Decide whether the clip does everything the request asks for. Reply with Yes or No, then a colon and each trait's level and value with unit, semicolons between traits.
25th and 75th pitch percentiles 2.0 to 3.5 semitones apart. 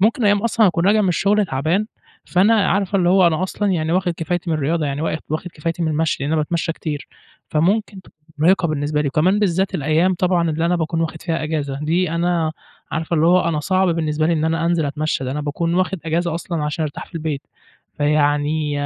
Yes: average, 3.0 semitones